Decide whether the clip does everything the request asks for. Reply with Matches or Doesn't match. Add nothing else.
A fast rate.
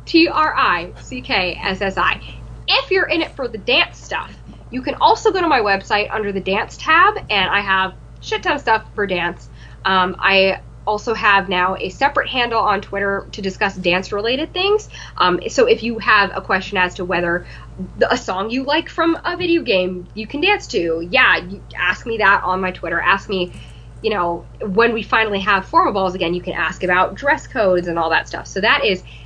Matches